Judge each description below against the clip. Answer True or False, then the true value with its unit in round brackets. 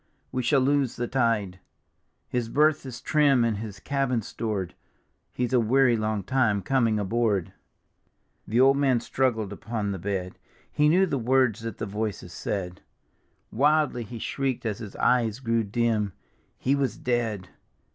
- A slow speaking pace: False (155 wpm)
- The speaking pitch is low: True (115 Hz)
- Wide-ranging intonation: False (3.9 semitones)